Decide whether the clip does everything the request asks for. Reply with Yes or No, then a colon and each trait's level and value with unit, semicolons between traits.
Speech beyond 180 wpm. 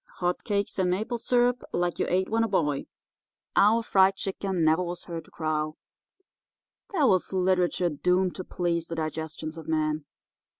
No: average, 165 wpm